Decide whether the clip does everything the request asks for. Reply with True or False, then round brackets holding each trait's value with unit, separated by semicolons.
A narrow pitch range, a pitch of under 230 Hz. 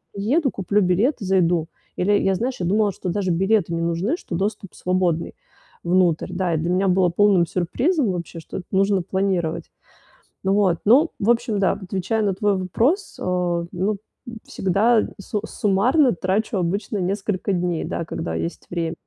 False (3.0 semitones; 190 Hz)